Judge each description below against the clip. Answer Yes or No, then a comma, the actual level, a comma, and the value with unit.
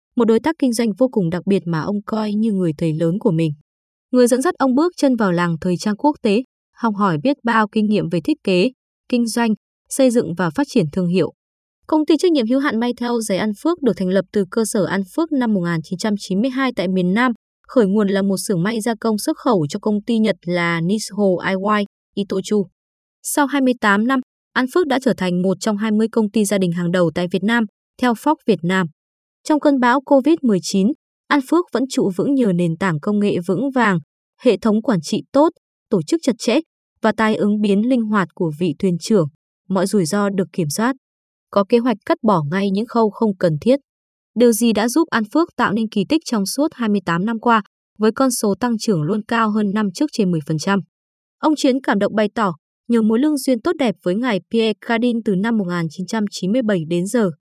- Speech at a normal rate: Yes, average, 225 wpm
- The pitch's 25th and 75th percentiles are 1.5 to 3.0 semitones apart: No, average, 4.3 semitones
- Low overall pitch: No, high, 215 Hz